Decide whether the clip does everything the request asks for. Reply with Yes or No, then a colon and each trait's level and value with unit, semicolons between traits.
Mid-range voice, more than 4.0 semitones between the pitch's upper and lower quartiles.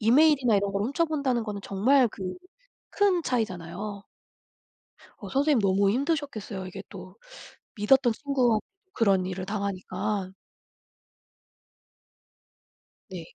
No: high, 215 Hz; wide, 5.6 semitones